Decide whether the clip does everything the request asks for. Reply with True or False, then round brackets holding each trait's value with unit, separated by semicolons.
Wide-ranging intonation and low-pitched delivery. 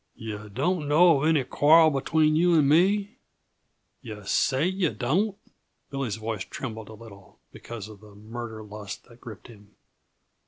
True (6.7 semitones; 120 Hz)